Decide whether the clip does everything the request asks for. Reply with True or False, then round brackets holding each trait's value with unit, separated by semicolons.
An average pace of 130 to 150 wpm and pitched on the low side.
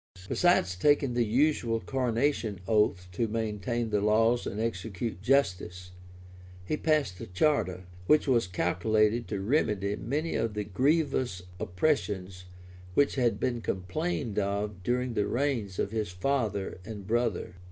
True (135 wpm; 110 Hz)